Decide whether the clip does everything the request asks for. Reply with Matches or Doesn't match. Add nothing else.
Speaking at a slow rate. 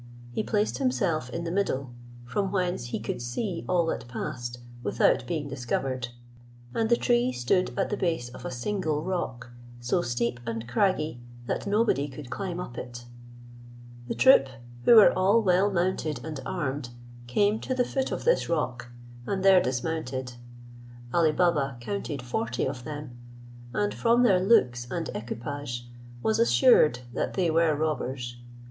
Doesn't match